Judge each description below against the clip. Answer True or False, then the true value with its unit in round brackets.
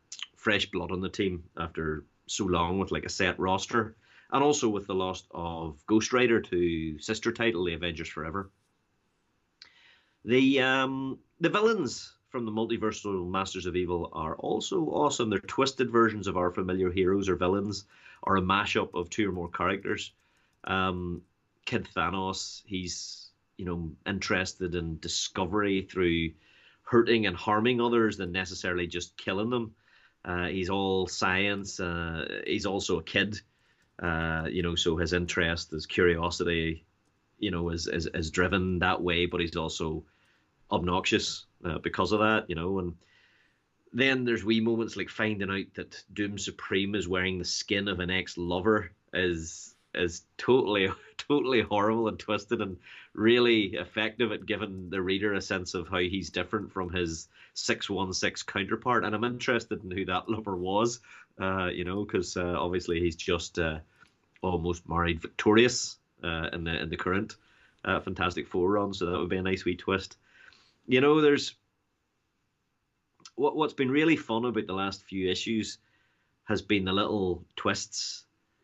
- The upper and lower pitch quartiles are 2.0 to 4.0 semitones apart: True (3.3 semitones)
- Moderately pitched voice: False (95 Hz)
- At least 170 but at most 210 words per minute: False (160 wpm)